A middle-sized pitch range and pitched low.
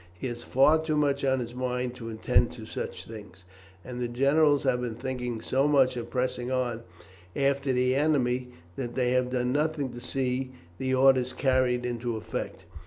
No: narrow, 1.6 semitones; low, 125 Hz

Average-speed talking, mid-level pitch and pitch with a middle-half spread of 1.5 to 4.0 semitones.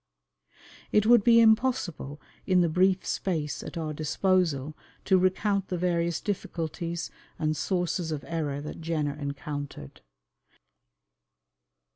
No: slow, 115 wpm; medium, 170 Hz; average, 3.7 semitones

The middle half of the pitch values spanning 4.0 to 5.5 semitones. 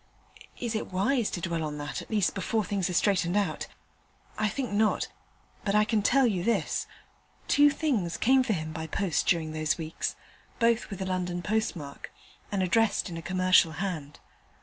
Yes: average, 4.4 semitones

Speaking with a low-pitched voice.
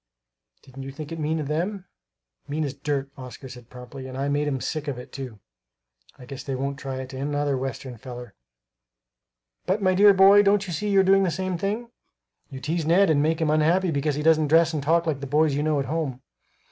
No: medium, 150 Hz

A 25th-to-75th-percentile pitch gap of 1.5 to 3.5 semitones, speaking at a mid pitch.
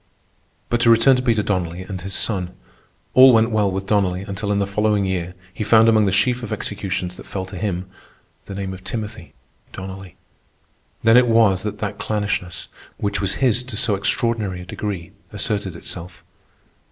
No: average, 2.9 semitones; low, 100 Hz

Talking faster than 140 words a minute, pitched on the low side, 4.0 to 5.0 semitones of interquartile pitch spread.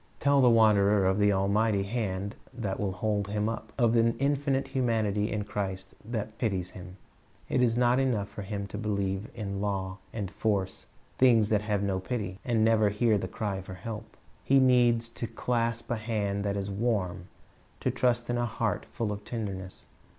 No: average, 185 wpm; low, 105 Hz; average, 2.8 semitones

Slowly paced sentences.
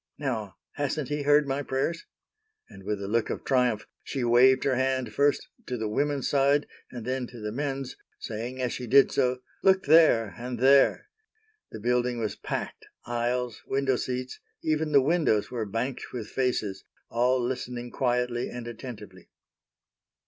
No: average, 155 wpm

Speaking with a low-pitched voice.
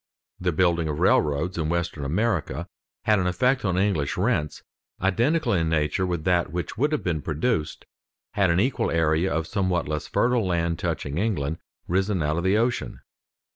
Yes: very low, 90 Hz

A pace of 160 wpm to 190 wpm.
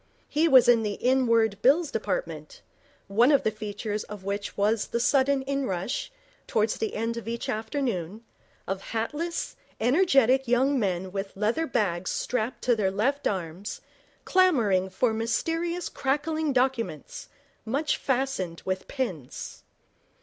No: slow, 135 wpm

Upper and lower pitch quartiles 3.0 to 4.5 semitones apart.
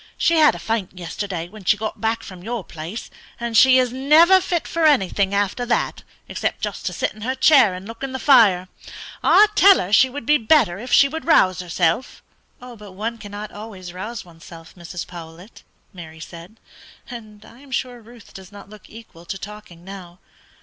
No: wide, 5.4 semitones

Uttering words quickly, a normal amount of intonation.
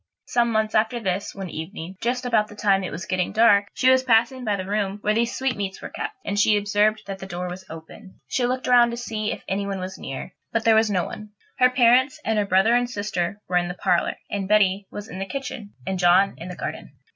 Yes: fast, 245 wpm; average, 3.4 semitones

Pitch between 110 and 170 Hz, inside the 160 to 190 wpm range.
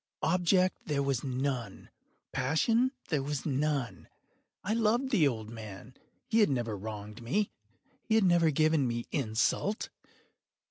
No: medium, 140 Hz; slow, 135 wpm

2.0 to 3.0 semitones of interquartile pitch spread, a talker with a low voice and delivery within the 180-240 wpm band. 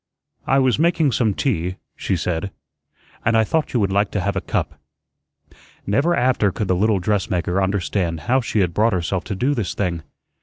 No: average, 4.7 semitones; low, 100 Hz; average, 190 wpm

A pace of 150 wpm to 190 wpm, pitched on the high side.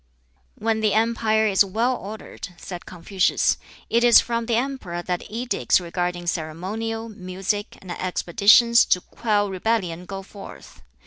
No: slow, 135 wpm; high, 205 Hz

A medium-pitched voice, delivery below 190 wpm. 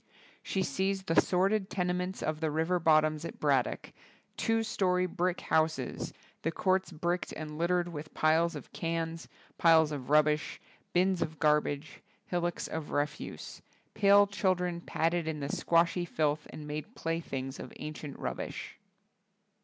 Yes: medium, 165 Hz; average, 145 wpm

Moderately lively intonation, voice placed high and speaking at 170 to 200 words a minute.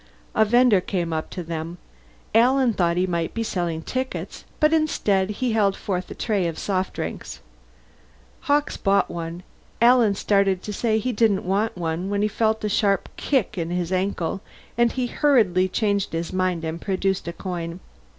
Yes: average, 4.0 semitones; high, 195 Hz; average, 175 wpm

